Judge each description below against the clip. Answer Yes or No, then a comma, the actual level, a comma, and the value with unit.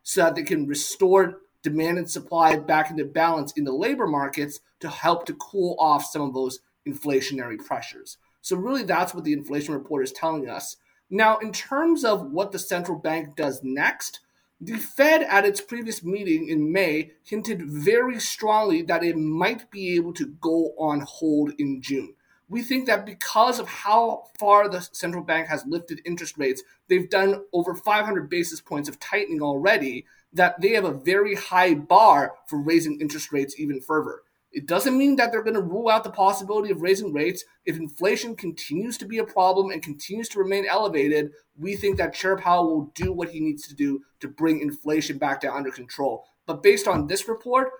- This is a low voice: No, medium, 180 Hz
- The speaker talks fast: No, average, 190 wpm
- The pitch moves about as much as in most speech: No, wide, 6.3 semitones